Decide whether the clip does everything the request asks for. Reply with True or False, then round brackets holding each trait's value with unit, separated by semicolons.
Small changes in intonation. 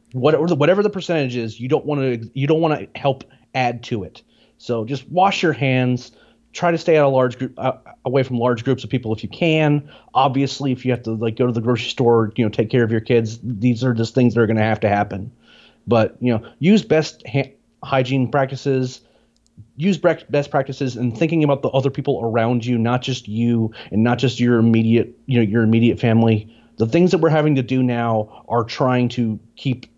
False (3.2 semitones)